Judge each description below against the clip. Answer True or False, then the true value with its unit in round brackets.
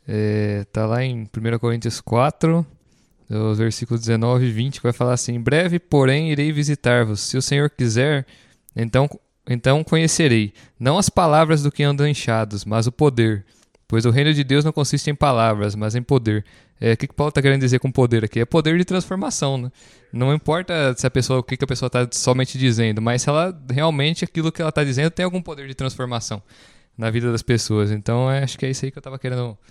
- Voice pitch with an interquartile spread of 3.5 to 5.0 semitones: True (3.9 semitones)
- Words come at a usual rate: False (210 wpm)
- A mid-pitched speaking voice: False (130 Hz)